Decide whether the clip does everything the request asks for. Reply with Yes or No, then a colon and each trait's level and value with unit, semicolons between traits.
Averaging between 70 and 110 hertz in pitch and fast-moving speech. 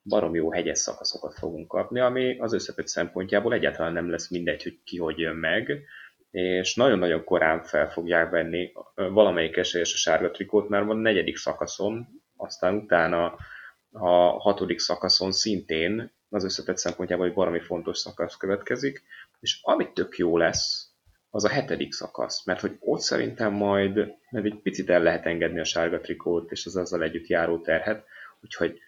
Yes: very low, 90 Hz; fast, 165 wpm